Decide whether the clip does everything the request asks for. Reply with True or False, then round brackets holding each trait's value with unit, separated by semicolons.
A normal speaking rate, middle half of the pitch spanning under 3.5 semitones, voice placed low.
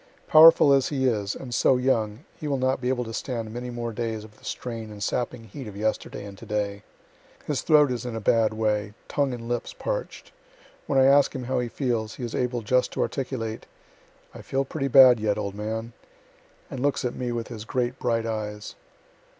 False (210 wpm; 3.1 semitones; 120 Hz)